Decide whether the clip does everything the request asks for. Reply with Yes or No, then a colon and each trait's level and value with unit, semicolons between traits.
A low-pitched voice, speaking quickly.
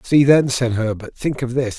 Yes: low, 125 Hz; fast, 235 wpm